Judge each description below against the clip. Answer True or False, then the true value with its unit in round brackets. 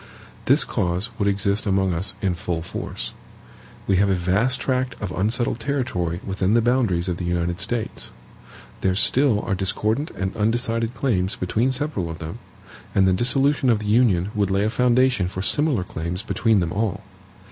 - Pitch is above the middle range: False (100 Hz)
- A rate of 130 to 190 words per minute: True (175 wpm)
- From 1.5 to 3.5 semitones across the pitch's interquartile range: False (4.7 semitones)